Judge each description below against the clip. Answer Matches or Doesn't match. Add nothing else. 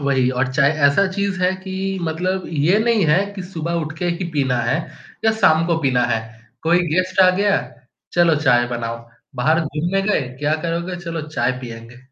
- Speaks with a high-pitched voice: Doesn't match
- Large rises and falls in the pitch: Matches